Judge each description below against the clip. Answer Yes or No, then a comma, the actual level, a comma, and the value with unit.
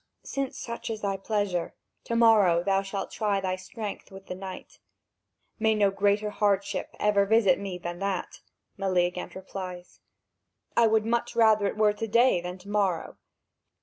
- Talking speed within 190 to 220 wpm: No, average, 160 wpm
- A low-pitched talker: No, high, 200 Hz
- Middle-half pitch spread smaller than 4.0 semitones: Yes, narrow, 2.5 semitones